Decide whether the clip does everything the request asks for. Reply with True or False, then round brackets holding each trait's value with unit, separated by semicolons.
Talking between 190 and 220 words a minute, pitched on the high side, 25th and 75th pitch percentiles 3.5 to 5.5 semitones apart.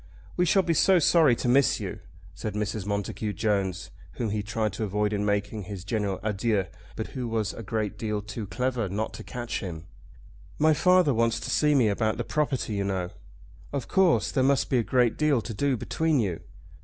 False (205 wpm; 110 Hz; 4.5 semitones)